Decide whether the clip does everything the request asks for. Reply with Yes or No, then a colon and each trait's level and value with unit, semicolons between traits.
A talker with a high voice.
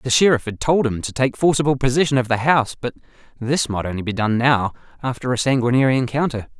No: low, 125 Hz